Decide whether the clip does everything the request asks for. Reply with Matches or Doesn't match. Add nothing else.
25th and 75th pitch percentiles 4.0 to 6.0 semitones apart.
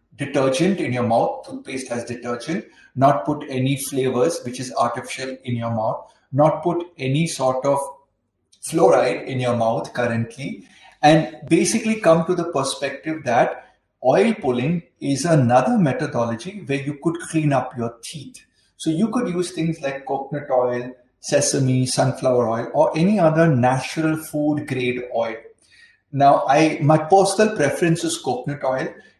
Matches